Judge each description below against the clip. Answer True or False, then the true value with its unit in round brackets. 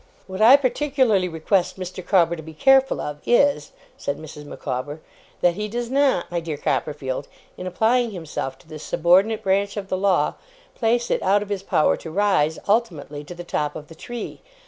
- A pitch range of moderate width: False (5.8 semitones)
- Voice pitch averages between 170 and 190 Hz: True (185 Hz)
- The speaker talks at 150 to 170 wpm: False (190 wpm)